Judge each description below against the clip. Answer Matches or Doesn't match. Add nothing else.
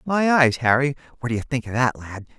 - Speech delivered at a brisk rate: Matches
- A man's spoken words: Matches